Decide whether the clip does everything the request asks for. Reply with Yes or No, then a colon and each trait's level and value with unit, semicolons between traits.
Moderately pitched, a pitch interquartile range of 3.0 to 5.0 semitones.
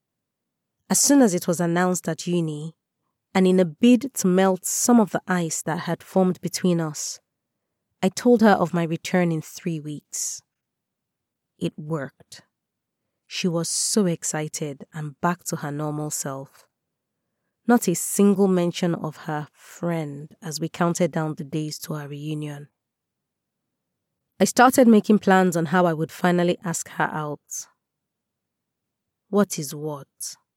Yes: medium, 170 Hz; average, 3.3 semitones